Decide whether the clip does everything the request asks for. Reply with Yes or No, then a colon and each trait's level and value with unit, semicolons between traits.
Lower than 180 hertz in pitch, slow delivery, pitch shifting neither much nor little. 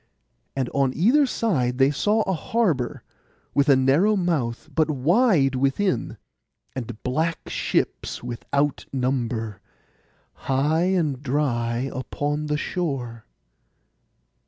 Yes: medium, 140 Hz; slow, 110 wpm; average, 4.7 semitones